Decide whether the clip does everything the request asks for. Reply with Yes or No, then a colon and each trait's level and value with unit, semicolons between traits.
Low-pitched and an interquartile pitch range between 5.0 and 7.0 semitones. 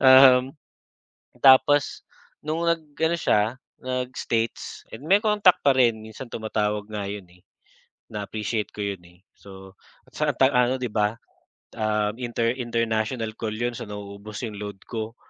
No: low, 110 Hz; average, 3.6 semitones